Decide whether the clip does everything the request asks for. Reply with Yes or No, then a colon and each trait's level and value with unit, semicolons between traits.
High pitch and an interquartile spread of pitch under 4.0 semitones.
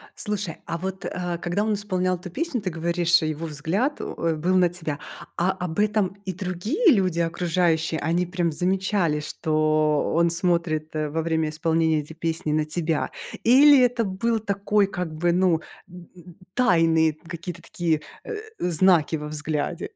No: medium, 170 Hz; average, 2.9 semitones